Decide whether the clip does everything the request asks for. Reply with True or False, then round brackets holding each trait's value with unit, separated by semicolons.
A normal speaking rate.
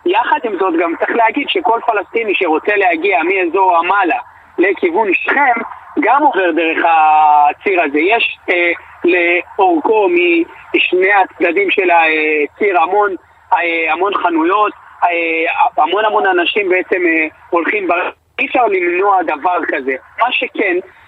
True (130 wpm)